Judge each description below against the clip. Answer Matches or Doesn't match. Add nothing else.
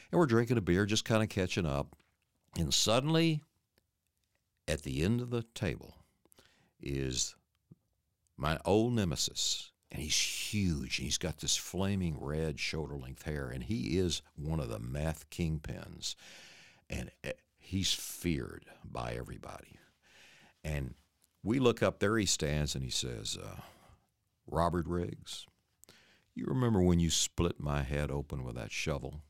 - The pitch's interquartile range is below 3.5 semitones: Doesn't match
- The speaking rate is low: Doesn't match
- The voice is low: Matches